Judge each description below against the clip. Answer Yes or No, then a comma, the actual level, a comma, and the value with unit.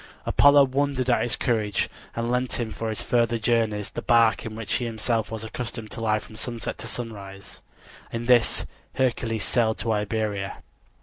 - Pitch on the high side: No, low, 115 Hz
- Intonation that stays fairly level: Yes, narrow, 1.8 semitones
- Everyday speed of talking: Yes, average, 175 wpm